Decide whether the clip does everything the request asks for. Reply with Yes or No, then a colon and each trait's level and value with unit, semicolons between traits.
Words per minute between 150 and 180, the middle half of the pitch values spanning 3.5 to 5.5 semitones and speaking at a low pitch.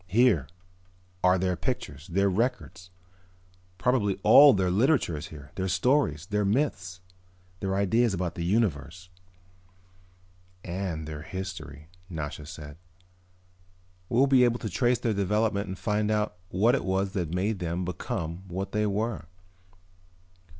No: slow, 135 wpm; average, 3.8 semitones; very low, 95 Hz